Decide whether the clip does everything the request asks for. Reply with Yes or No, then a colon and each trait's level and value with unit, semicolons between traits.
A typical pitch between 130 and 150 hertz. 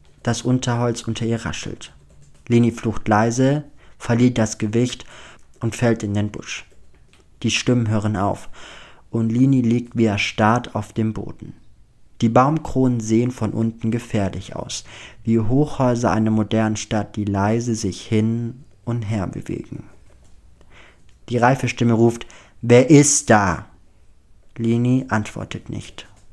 No: low, 115 Hz